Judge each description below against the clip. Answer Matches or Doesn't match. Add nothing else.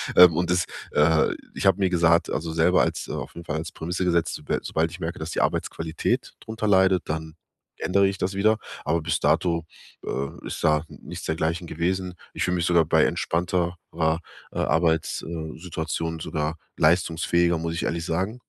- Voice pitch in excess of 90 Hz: Doesn't match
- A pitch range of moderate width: Doesn't match